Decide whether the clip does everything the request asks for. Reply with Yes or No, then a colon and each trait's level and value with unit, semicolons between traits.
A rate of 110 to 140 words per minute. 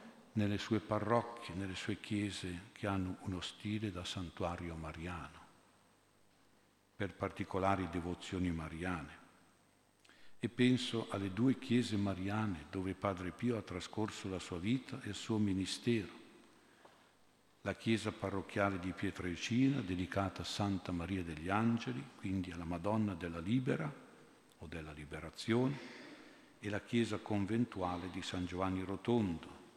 Yes: average, 125 wpm